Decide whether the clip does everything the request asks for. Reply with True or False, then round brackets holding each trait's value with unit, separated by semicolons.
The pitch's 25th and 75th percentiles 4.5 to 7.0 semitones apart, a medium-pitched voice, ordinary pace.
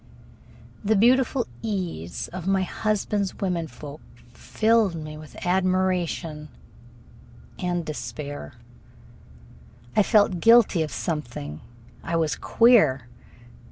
False (5.2 semitones; 180 Hz; 95 wpm)